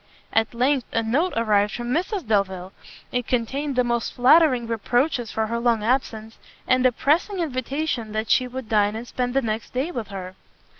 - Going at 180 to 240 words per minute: Yes, average, 185 wpm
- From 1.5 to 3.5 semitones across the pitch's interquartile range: Yes, average, 3.1 semitones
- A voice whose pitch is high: Yes, high, 240 Hz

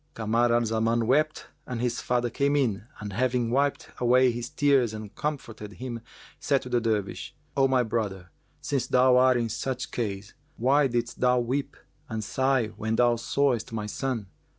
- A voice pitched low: Yes, low, 120 Hz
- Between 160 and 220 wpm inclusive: Yes, average, 175 wpm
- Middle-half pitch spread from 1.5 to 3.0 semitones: Yes, narrow, 2.6 semitones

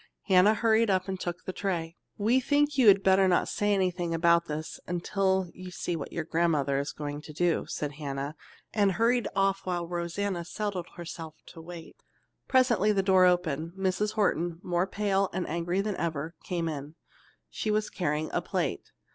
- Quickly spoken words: No, average, 180 wpm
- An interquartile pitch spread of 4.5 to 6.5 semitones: No, average, 3.1 semitones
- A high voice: No, medium, 180 Hz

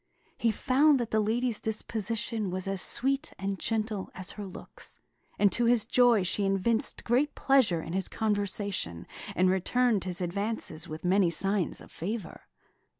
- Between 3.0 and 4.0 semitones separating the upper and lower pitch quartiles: Yes, average, 3.7 semitones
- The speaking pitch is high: Yes, high, 205 Hz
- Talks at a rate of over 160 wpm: No, average, 155 wpm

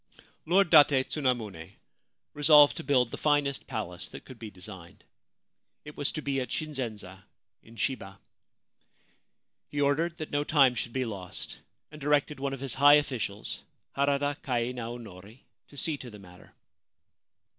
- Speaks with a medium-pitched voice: No, low, 130 Hz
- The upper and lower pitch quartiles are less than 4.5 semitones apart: No, average, 4.8 semitones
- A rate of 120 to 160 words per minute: Yes, average, 150 wpm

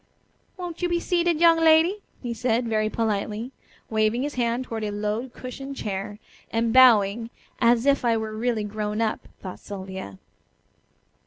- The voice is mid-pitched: No, high, 230 Hz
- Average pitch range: Yes, average, 3.5 semitones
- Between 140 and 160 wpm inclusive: Yes, average, 155 wpm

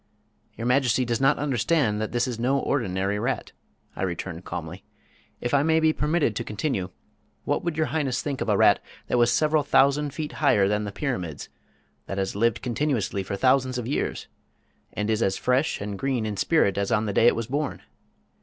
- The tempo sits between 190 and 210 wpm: Yes, average, 200 wpm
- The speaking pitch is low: Yes, low, 120 Hz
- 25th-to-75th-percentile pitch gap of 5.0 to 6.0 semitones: Yes, wide, 5.5 semitones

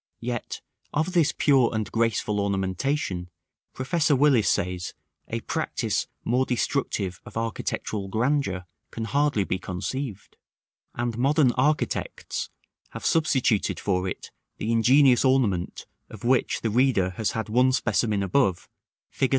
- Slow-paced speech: Yes, slow, 125 wpm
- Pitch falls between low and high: No, low, 115 Hz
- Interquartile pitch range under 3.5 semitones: No, average, 5.3 semitones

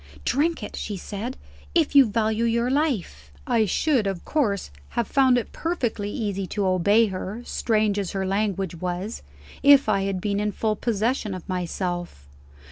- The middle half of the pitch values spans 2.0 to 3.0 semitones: No, average, 3.8 semitones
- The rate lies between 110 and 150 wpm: No, average, 165 wpm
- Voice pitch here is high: Yes, high, 210 Hz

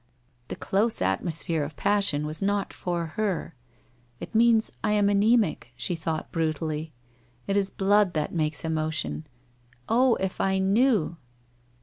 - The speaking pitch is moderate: Yes, medium, 180 Hz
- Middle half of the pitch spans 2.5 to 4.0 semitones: No, average, 4.6 semitones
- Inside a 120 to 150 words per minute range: Yes, average, 140 wpm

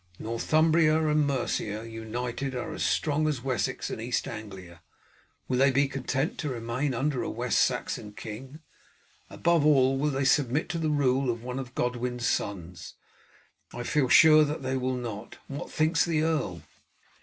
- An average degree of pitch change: Yes, average, 4.2 semitones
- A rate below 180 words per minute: Yes, average, 165 wpm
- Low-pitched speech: Yes, low, 130 Hz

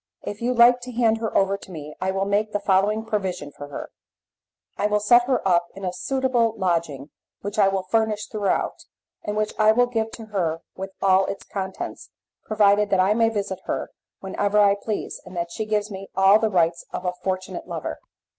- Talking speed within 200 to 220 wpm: Yes, fast, 205 wpm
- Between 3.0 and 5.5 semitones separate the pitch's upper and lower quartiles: No, narrow, 2.5 semitones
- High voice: Yes, high, 200 Hz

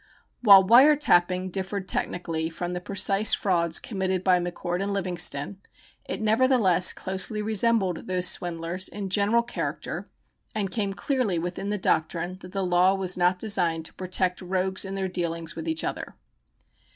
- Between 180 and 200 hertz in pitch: Yes, medium, 185 Hz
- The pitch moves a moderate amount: No, narrow, 2.2 semitones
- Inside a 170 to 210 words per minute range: No, average, 155 wpm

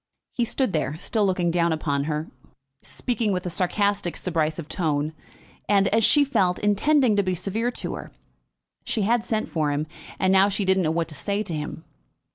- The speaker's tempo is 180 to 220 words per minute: Yes, average, 190 wpm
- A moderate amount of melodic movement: Yes, average, 4.6 semitones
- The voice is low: No, medium, 185 Hz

